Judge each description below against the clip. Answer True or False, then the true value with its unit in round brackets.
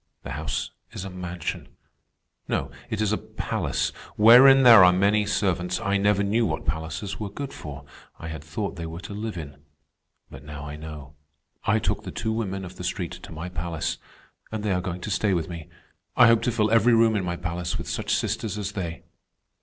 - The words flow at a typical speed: False (210 wpm)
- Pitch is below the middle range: True (95 Hz)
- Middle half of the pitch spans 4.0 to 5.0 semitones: True (4.5 semitones)